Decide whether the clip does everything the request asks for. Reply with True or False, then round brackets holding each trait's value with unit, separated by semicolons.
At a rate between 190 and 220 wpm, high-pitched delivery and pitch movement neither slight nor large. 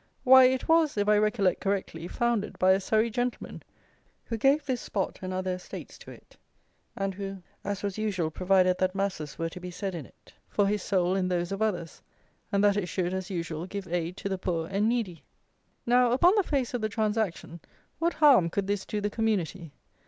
True (205 wpm; 200 Hz; 3.4 semitones)